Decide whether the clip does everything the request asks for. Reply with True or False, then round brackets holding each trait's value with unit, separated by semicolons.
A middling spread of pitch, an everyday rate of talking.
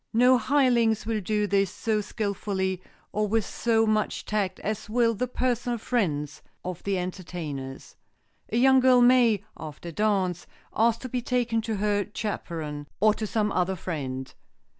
True (3.9 semitones; 160 wpm)